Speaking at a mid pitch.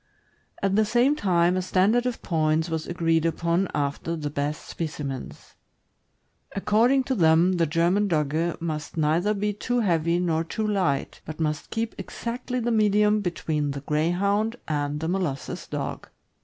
Yes: medium, 170 Hz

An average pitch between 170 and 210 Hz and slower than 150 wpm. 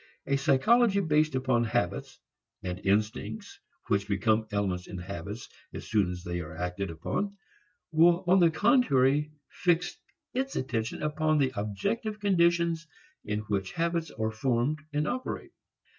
No: low, 130 Hz; average, 140 wpm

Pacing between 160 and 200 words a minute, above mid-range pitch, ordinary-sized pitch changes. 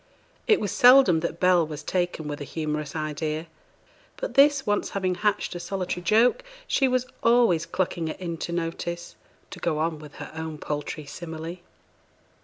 No: average, 165 wpm; medium, 170 Hz; average, 4.2 semitones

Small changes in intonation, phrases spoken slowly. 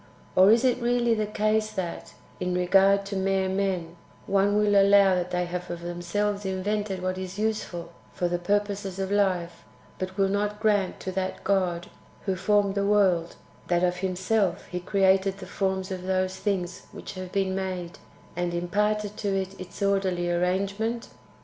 No: narrow, 2.1 semitones; average, 170 wpm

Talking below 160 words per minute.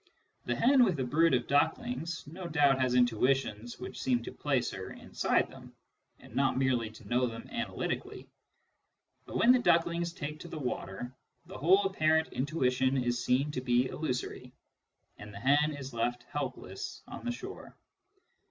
No: average, 165 wpm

